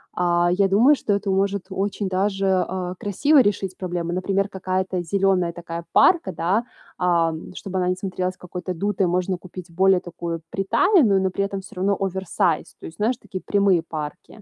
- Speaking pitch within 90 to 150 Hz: No, medium, 185 Hz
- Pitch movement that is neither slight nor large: No, narrow, 1.9 semitones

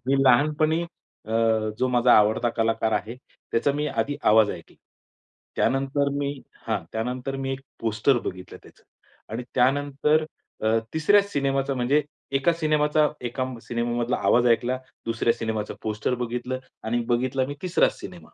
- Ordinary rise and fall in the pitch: Yes, average, 3.5 semitones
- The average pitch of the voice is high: No, low, 130 Hz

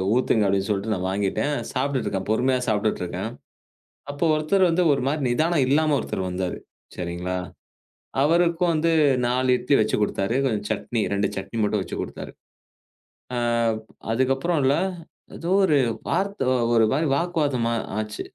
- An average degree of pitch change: No, wide, 6.8 semitones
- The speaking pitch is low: Yes, low, 130 Hz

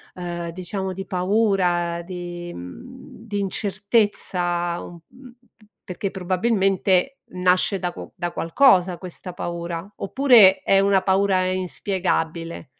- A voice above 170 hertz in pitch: Yes, medium, 185 Hz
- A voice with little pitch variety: Yes, narrow, 2.2 semitones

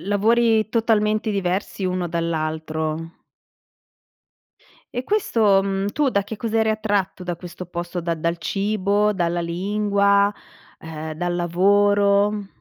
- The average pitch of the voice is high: Yes, high, 195 Hz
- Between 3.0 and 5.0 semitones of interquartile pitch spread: Yes, average, 3.4 semitones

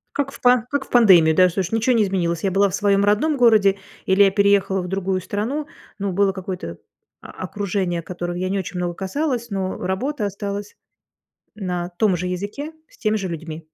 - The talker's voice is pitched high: Yes, high, 195 Hz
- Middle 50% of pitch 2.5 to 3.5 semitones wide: Yes, average, 2.8 semitones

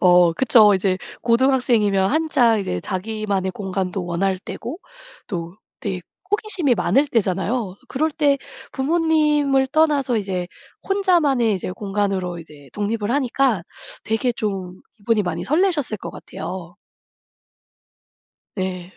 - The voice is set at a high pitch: Yes, high, 215 Hz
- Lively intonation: Yes, wide, 6.5 semitones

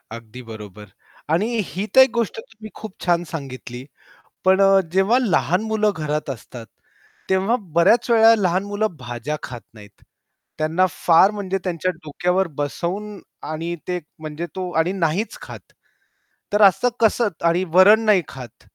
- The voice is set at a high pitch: No, medium, 180 Hz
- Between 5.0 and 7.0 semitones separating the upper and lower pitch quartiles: Yes, wide, 5.4 semitones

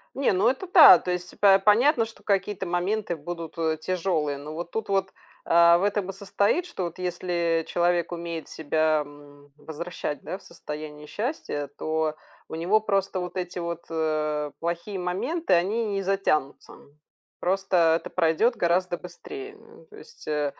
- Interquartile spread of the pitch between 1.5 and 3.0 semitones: No, average, 3.6 semitones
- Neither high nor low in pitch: Yes, medium, 175 Hz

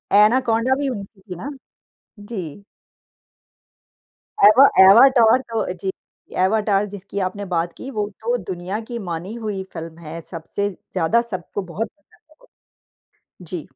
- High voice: Yes, high, 200 Hz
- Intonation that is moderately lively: Yes, average, 3.7 semitones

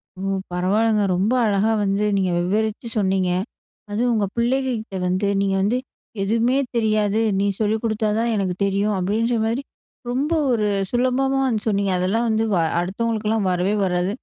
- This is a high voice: Yes, high, 215 Hz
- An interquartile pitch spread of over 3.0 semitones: No, average, 2.7 semitones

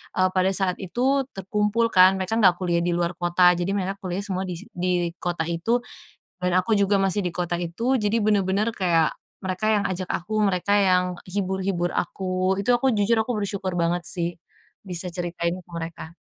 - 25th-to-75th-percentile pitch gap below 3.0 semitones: Yes, narrow, 2.5 semitones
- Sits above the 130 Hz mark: Yes, medium, 185 Hz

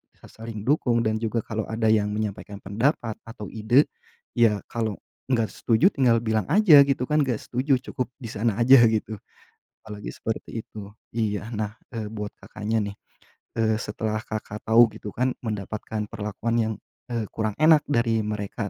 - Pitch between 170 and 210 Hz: No, low, 110 Hz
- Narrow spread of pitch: Yes, narrow, 1.8 semitones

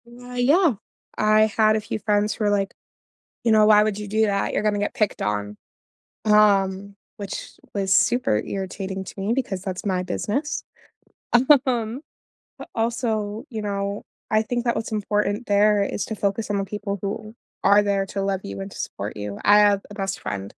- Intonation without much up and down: Yes, narrow, 1.8 semitones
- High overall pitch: Yes, high, 205 Hz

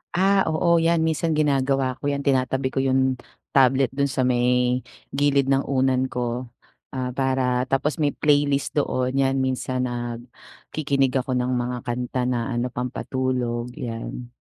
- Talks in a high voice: No, low, 130 Hz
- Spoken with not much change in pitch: Yes, narrow, 1.9 semitones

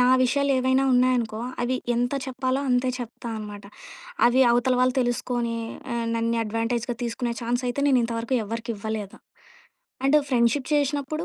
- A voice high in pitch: Yes, high, 245 Hz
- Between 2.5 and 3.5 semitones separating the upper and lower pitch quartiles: No, narrow, 2.0 semitones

